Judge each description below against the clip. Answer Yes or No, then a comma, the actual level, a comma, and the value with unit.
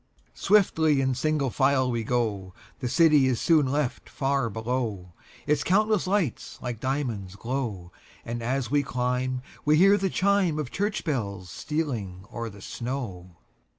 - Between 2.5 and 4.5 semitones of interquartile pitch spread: No, average, 4.9 semitones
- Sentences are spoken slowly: Yes, slow, 130 wpm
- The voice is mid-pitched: No, low, 130 Hz